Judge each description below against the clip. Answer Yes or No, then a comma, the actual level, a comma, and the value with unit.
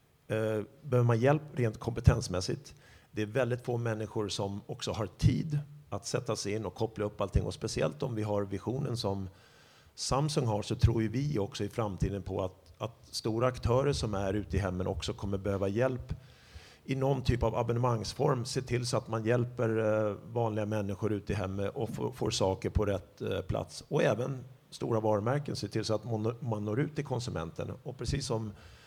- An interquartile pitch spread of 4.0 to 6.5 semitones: No, average, 3.4 semitones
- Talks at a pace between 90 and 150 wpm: No, average, 190 wpm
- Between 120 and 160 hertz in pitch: No, low, 110 Hz